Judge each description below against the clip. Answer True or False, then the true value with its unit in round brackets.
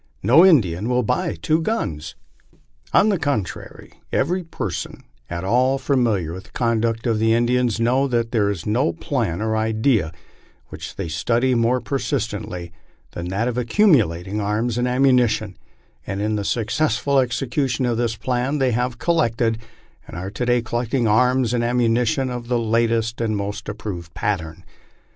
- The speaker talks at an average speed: True (165 wpm)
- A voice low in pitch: True (115 Hz)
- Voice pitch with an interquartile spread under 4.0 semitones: True (3.1 semitones)